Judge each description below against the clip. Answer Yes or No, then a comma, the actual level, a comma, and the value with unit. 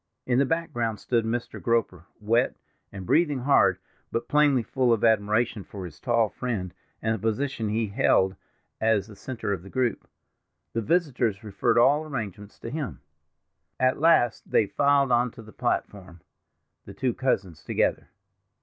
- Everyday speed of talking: Yes, average, 155 wpm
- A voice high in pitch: No, low, 115 Hz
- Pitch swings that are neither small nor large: Yes, average, 4.0 semitones